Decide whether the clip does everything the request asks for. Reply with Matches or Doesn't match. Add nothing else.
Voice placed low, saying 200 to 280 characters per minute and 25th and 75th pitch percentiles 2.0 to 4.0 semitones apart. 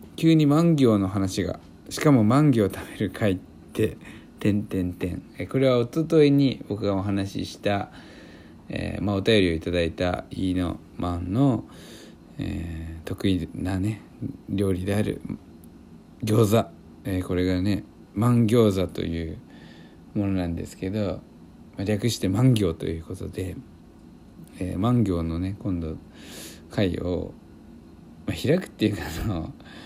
Matches